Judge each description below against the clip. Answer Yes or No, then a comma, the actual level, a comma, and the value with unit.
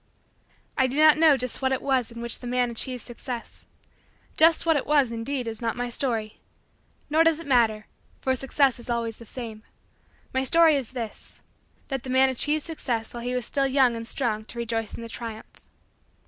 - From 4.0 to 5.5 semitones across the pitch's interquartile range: No, average, 2.9 semitones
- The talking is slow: No, average, 200 wpm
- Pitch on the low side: No, very high, 250 Hz